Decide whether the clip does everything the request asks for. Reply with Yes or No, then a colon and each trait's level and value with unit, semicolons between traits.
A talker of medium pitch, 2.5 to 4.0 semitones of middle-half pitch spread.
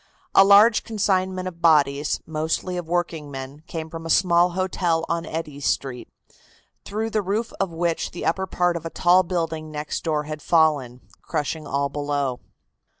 Yes: medium, 165 Hz; average, 3.5 semitones